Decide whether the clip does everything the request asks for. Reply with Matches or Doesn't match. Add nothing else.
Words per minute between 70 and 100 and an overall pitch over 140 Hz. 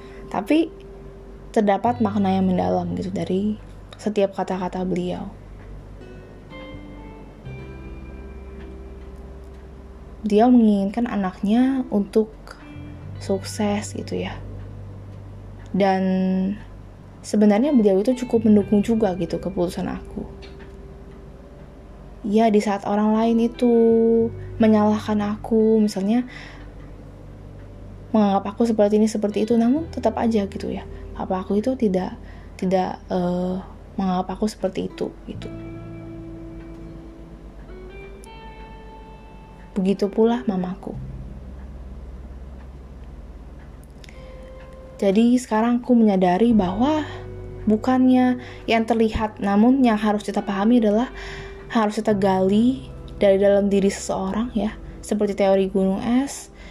Matches